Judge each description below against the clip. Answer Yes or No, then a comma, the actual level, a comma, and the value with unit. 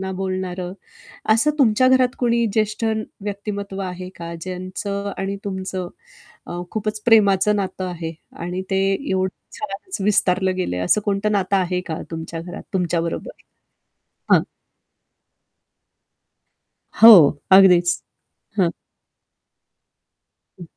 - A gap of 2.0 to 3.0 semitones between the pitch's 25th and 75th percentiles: Yes, average, 2.7 semitones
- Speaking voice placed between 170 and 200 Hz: Yes, high, 190 Hz